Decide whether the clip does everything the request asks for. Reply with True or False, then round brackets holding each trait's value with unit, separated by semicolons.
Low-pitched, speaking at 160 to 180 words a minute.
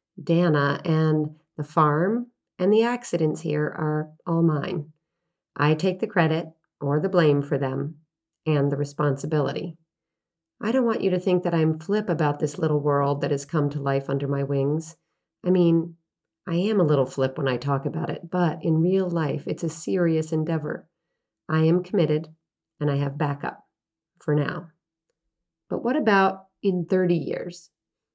False (160 Hz; 170 wpm)